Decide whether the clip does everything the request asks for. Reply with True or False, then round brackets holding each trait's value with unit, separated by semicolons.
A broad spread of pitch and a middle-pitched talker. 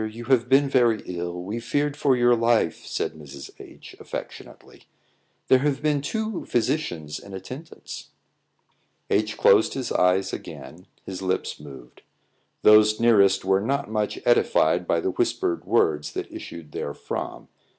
False (6.9 semitones; 110 Hz)